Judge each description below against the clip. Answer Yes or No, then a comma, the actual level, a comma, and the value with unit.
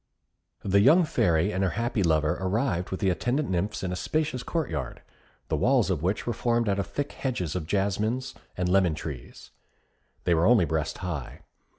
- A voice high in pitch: No, very low, 95 Hz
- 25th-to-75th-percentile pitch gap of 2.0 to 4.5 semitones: No, wide, 5.6 semitones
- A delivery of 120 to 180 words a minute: No, average, 190 wpm